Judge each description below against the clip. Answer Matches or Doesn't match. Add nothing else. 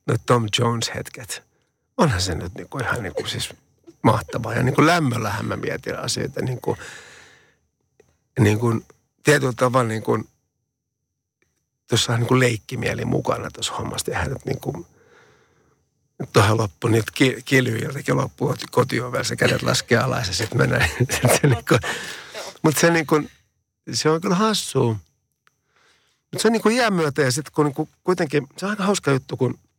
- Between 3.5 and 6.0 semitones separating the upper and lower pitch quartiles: Matches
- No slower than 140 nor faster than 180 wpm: Matches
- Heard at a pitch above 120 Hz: Matches